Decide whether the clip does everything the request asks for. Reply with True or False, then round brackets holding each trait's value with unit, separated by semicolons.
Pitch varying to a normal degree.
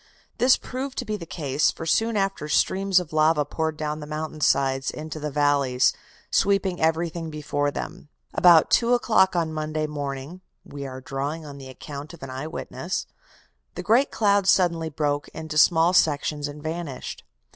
True (3.6 semitones)